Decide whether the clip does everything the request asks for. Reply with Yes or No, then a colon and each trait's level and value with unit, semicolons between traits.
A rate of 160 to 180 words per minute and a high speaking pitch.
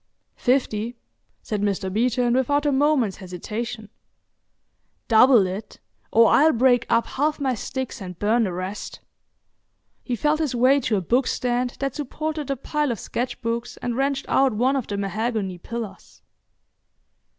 No: average, 150 wpm; high, 240 Hz